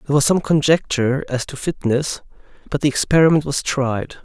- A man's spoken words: Yes, male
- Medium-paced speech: Yes, average, 170 wpm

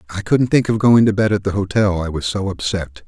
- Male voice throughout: Yes, male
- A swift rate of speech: Yes, fast, 275 wpm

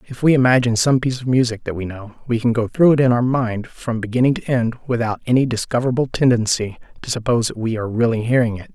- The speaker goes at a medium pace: No, fast, 235 wpm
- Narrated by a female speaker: No, male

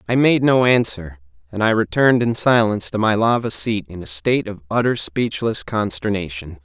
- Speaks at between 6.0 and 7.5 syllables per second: No, 5.3 syllables/s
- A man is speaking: Yes, male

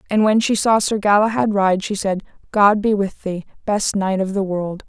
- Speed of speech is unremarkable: No, fast, 220 wpm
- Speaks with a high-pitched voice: Yes, high, 200 Hz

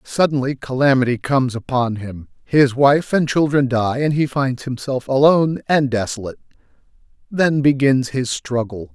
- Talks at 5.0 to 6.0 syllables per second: No, 4.8 syllables/s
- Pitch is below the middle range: Yes, low, 130 Hz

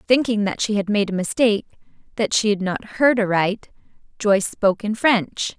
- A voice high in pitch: Yes, high, 210 Hz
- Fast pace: No, average, 185 wpm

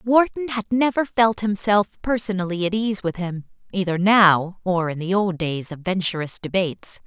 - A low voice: No, high, 195 Hz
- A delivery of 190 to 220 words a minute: No, average, 170 wpm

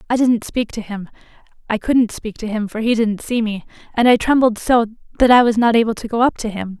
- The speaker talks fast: Yes, fast, 245 wpm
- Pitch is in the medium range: No, high, 225 Hz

